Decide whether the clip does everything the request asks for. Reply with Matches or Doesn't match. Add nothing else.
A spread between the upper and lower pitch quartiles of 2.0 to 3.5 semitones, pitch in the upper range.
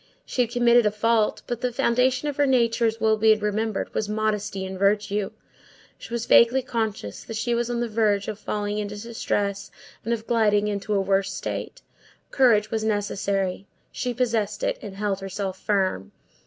Matches